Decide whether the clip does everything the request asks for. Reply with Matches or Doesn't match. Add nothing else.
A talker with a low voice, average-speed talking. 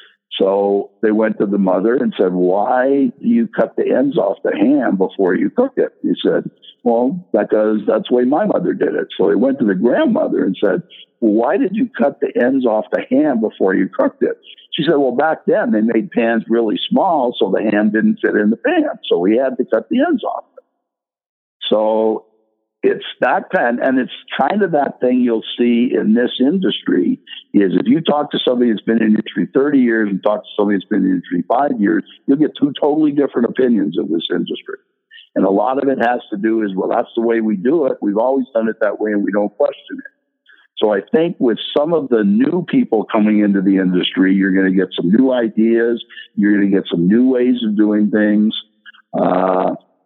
Doesn't match